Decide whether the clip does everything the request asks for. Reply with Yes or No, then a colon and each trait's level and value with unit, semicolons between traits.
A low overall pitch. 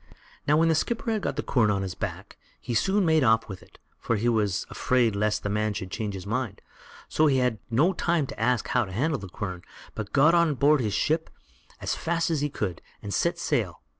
Yes: low, 120 Hz